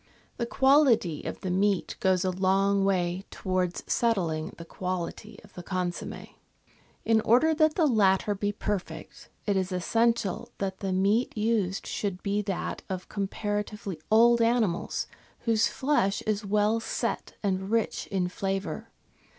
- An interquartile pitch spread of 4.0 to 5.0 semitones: No, average, 3.1 semitones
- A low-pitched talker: No, high, 200 Hz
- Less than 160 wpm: Yes, average, 140 wpm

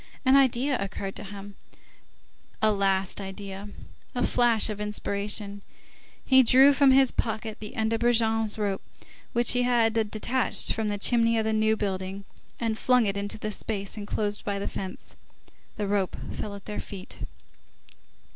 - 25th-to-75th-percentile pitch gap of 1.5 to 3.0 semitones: Yes, narrow, 2.6 semitones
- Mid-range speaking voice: No, high, 215 Hz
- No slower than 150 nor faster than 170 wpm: Yes, average, 160 wpm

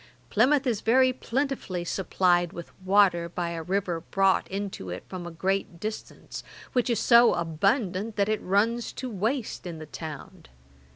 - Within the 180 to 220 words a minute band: No, average, 160 wpm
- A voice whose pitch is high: Yes, high, 195 Hz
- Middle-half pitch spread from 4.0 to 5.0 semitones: Yes, average, 4.7 semitones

